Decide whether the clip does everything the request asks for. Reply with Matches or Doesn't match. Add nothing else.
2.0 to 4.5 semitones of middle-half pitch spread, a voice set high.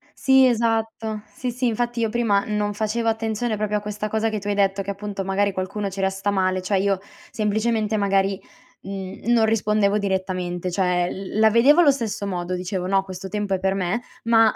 Matches